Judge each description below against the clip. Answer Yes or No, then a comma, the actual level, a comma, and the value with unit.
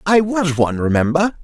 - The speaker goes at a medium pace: Yes, average, 165 wpm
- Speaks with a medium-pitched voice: Yes, medium, 160 Hz